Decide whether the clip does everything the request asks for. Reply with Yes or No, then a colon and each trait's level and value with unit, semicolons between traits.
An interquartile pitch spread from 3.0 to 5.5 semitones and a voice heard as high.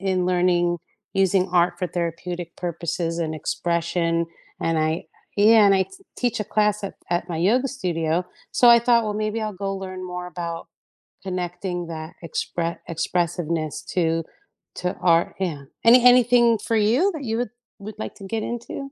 No: average, 4.0 semitones; medium, 180 Hz